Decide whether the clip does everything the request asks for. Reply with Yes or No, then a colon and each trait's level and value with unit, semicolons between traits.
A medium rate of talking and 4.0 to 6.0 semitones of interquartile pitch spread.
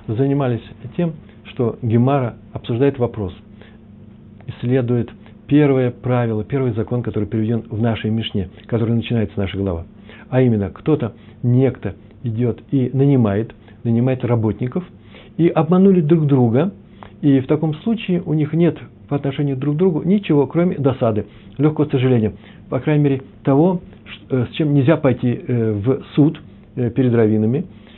Yes: average, 135 wpm; average, 4.6 semitones